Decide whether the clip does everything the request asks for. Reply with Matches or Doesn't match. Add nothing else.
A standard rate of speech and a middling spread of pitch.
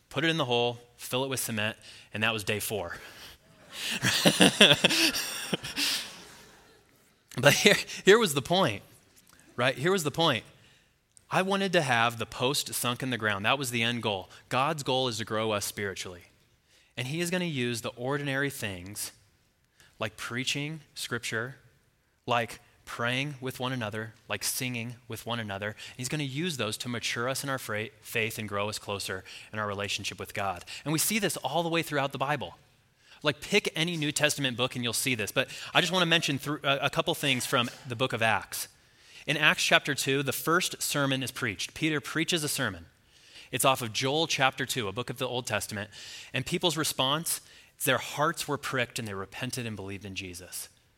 Matches